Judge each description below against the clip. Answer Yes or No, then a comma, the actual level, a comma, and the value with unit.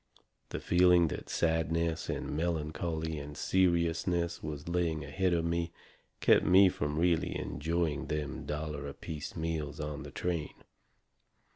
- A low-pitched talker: Yes, very low, 80 Hz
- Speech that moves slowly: Yes, slow, 130 wpm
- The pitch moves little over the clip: Yes, narrow, 2.2 semitones